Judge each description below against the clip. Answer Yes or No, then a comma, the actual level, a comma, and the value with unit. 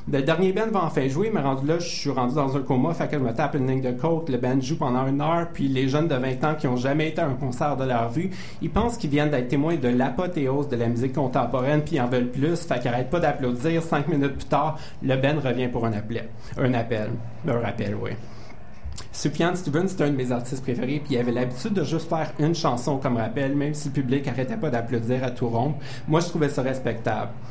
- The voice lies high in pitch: No, low, 135 Hz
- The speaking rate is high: Yes, fast, 255 wpm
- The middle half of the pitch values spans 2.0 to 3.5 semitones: No, average, 3.9 semitones